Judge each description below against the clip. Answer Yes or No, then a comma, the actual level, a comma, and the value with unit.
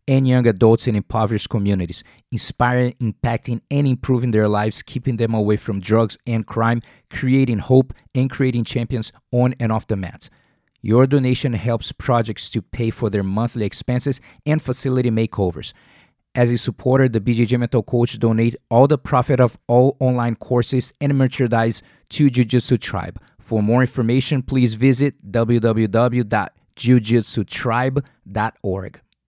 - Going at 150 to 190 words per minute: No, average, 140 wpm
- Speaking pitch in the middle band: No, low, 120 Hz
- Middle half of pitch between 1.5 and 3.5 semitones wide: Yes, narrow, 2.5 semitones